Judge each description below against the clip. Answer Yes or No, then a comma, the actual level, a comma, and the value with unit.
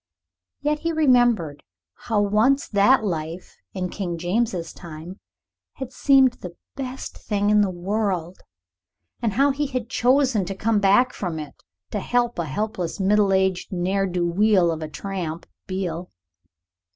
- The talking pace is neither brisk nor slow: Yes, average, 150 wpm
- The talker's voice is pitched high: Yes, high, 200 Hz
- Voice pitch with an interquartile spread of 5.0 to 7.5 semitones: Yes, wide, 5.4 semitones